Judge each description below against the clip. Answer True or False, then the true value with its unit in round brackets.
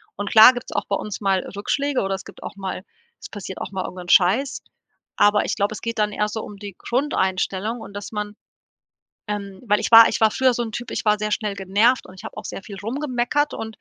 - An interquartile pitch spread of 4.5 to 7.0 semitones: False (2.7 semitones)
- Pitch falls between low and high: False (210 Hz)